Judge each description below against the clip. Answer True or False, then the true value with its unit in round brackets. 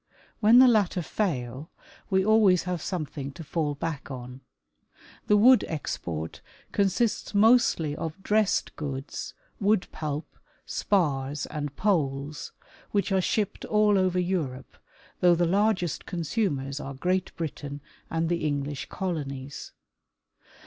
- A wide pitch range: True (5.8 semitones)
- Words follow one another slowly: True (120 wpm)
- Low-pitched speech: False (165 Hz)